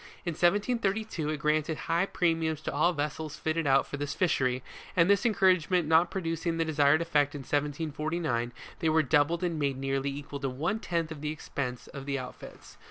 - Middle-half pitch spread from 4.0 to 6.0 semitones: No, average, 3.0 semitones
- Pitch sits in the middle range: Yes, medium, 155 Hz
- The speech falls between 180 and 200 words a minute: Yes, average, 190 wpm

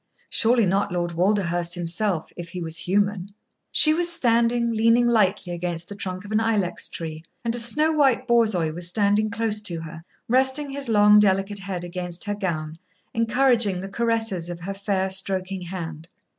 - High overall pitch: Yes, high, 200 Hz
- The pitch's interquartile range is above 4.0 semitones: Yes, average, 4.5 semitones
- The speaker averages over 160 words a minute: Yes, average, 170 wpm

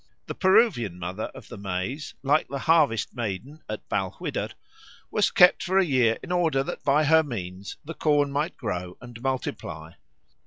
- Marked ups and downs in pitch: Yes, wide, 7.2 semitones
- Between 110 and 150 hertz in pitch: Yes, low, 135 Hz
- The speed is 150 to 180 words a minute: Yes, average, 165 wpm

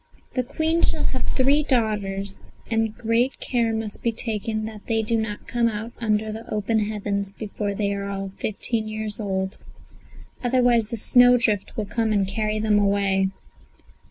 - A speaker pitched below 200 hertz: No, high, 215 Hz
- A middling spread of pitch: No, narrow, 2.3 semitones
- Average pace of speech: Yes, average, 160 wpm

